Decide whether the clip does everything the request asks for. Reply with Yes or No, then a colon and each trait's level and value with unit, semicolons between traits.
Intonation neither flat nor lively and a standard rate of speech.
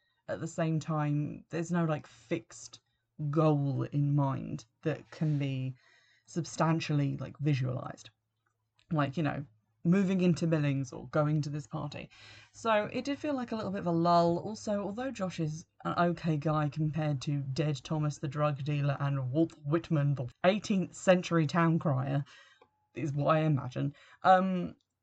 Yes: average, 3.4 semitones; average, 160 wpm